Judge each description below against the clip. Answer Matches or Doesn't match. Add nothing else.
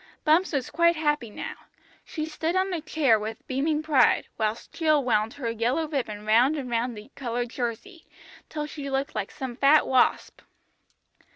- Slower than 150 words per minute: Doesn't match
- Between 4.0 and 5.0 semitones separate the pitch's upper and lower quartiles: Matches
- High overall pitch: Matches